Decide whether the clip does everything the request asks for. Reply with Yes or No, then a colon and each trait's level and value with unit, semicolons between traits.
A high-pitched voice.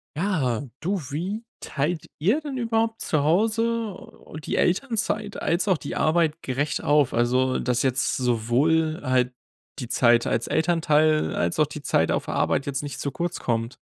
No: medium, 155 Hz